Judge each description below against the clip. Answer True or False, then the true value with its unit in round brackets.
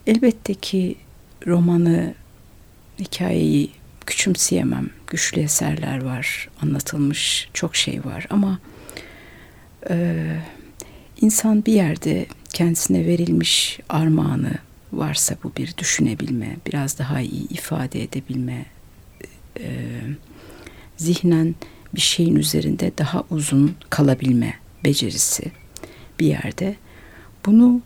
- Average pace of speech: False (90 wpm)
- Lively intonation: True (5.8 semitones)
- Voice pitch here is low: False (150 Hz)